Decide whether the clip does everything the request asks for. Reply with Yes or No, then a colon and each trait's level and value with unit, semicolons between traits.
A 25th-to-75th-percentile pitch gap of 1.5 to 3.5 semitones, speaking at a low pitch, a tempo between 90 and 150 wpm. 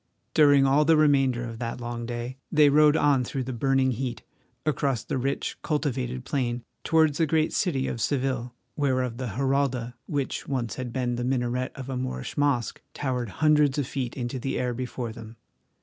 No: narrow, 2.6 semitones; low, 130 Hz; average, 180 wpm